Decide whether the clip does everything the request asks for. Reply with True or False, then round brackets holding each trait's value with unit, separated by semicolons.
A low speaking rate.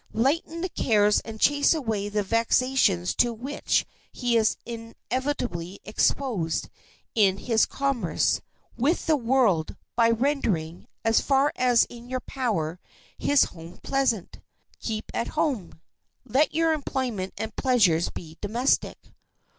True (130 wpm)